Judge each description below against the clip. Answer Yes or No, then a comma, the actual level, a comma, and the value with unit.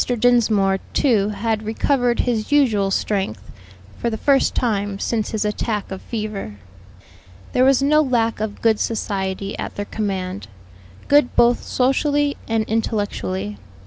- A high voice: Yes, high, 220 Hz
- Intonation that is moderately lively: Yes, average, 3.6 semitones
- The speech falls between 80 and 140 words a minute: Yes, slow, 135 wpm